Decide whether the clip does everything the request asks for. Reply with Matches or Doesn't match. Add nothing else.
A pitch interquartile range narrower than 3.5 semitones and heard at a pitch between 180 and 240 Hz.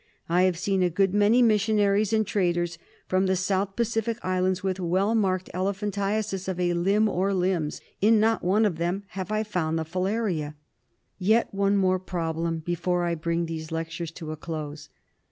Matches